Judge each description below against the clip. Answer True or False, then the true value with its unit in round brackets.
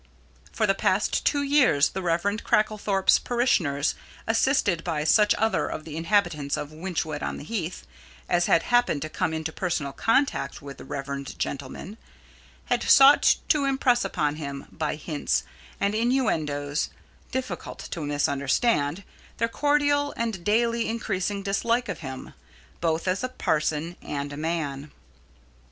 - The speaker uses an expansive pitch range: True (7.4 semitones)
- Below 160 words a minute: True (140 wpm)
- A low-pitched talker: False (175 Hz)